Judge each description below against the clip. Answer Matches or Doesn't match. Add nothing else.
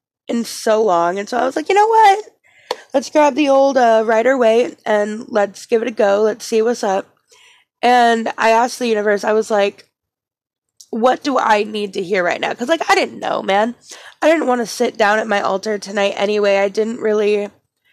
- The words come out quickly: Matches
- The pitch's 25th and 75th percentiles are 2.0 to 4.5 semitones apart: Matches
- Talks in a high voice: Matches